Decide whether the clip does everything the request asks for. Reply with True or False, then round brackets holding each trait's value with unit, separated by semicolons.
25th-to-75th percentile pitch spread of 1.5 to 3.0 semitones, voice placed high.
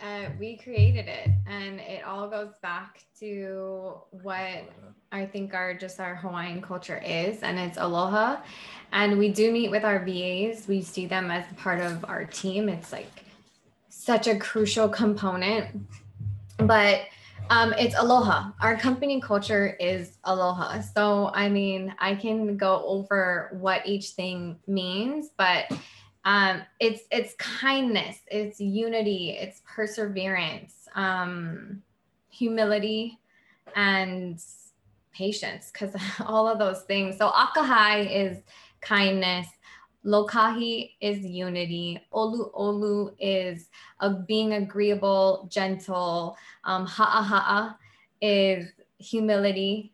True (2.5 semitones; 200 Hz)